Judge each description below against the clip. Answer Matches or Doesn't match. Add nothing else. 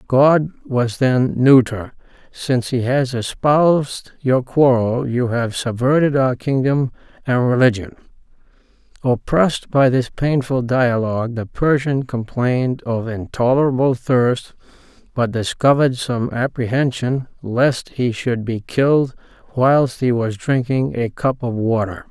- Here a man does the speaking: Matches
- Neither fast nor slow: Doesn't match